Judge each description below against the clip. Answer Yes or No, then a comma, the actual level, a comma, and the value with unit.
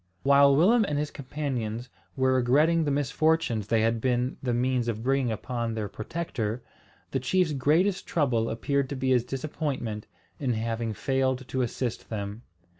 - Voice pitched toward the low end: Yes, low, 130 Hz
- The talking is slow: No, average, 160 wpm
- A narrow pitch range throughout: No, average, 3.6 semitones